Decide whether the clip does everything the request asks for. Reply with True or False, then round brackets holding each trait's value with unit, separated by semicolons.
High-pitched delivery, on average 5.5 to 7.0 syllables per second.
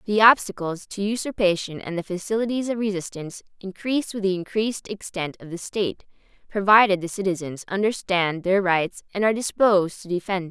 True (195 Hz; 5.8 syllables/s)